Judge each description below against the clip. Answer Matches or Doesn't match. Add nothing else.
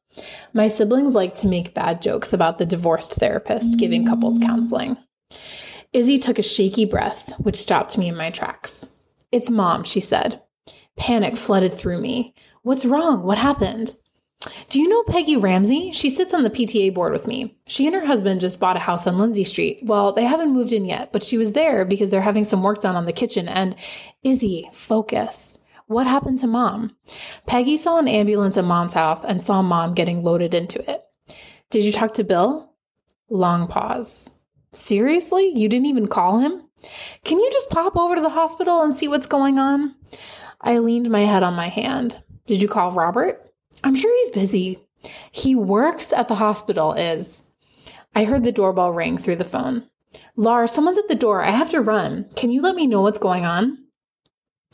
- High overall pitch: Matches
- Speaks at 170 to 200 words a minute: Matches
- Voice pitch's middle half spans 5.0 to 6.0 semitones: Matches